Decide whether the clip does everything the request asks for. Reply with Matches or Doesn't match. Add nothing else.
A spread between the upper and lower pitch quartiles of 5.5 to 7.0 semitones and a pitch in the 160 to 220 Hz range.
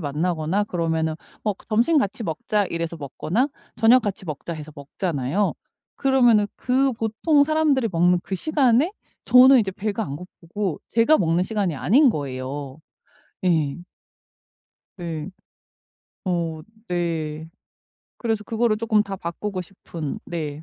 Matches